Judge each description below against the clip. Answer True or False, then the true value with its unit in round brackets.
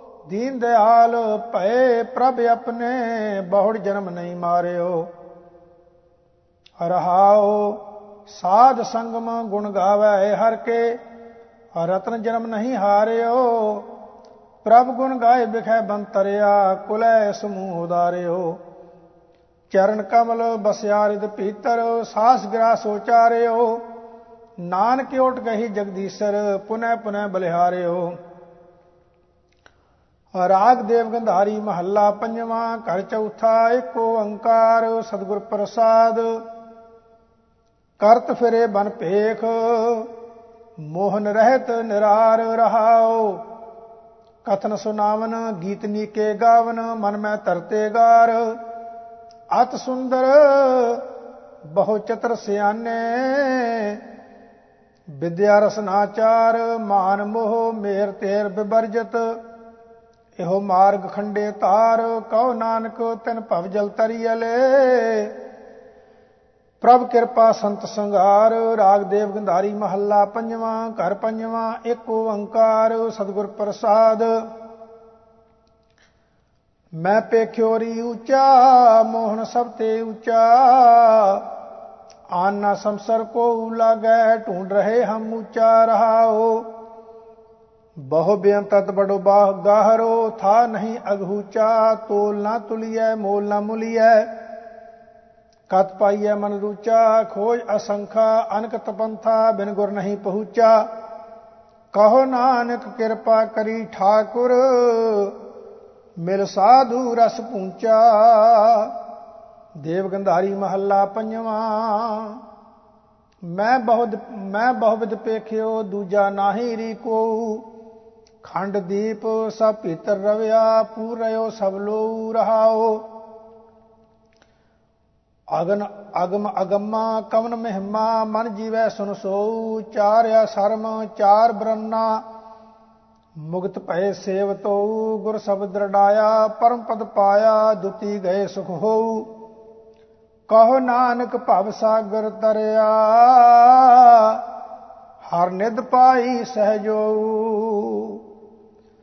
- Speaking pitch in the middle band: False (220 Hz)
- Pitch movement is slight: True (1.9 semitones)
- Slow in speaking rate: True (85 wpm)